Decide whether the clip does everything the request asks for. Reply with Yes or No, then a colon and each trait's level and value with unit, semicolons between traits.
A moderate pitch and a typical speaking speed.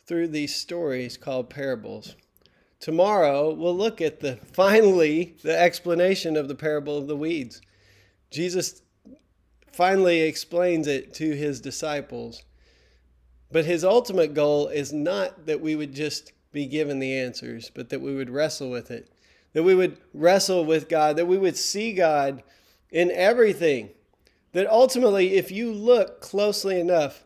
Yes: medium, 155 Hz; average, 150 wpm